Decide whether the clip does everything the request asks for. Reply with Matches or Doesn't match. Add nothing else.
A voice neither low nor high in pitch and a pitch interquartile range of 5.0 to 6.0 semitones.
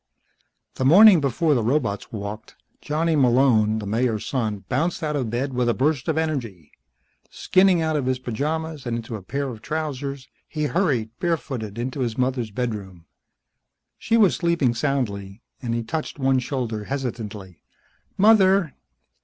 Doesn't match